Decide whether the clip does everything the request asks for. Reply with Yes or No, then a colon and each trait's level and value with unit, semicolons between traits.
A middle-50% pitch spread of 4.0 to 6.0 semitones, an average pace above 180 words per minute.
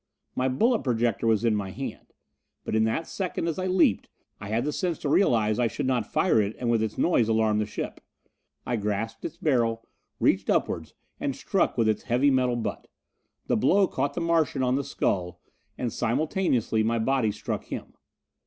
Yes: average, 4.5 semitones; average, 190 wpm